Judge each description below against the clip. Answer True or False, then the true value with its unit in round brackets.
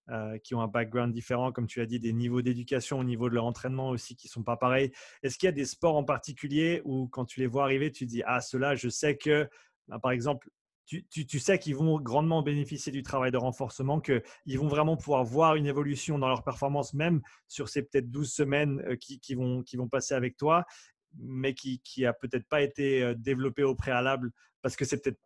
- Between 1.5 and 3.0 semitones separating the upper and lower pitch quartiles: True (2.7 semitones)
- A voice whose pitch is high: False (135 Hz)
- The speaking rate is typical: False (235 wpm)